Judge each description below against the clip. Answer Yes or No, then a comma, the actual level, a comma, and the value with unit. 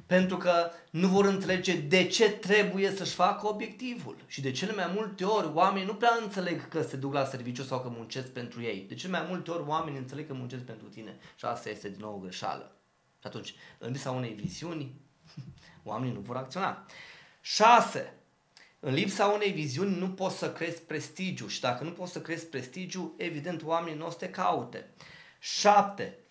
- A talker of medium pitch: Yes, medium, 170 Hz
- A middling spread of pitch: No, wide, 5.8 semitones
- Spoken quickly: Yes, fast, 185 wpm